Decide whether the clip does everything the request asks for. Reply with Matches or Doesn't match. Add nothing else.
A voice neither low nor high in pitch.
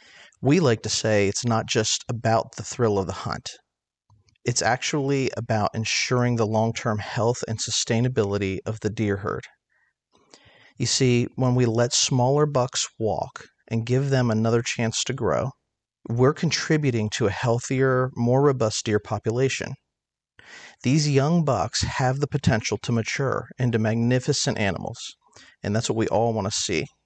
Doesn't match